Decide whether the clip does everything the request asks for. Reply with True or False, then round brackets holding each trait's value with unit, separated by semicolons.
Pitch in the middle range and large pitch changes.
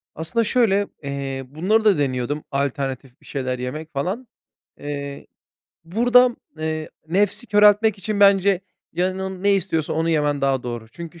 True (165 Hz; 6.3 semitones)